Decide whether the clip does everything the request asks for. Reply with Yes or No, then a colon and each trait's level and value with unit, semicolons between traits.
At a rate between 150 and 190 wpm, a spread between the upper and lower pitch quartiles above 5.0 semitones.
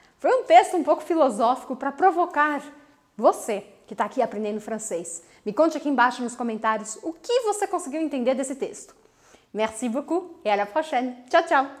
Yes: average, 180 wpm; wide, 5.5 semitones